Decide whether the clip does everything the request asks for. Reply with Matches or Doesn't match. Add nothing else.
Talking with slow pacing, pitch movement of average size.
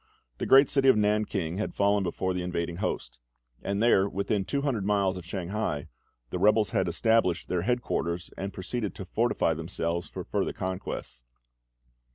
Doesn't match